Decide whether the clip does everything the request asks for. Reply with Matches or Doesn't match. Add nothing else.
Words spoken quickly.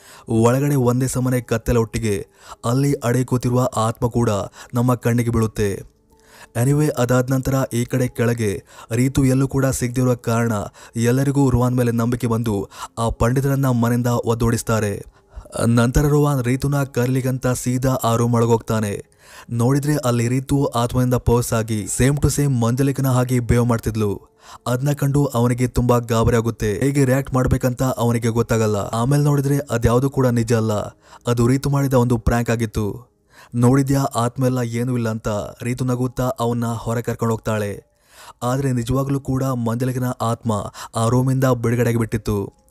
Matches